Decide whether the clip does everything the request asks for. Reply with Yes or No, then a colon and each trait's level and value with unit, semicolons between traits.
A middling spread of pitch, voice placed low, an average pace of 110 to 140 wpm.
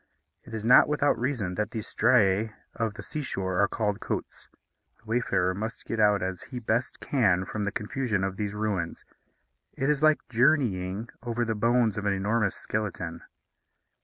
No: average, 3.4 semitones; low, 110 Hz; average, 175 wpm